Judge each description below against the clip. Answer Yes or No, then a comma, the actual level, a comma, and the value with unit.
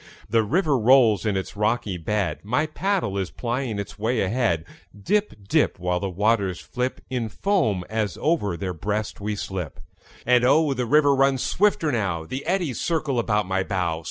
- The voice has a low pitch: Yes, low, 110 Hz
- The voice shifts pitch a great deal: Yes, wide, 5.8 semitones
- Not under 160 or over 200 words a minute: Yes, average, 175 wpm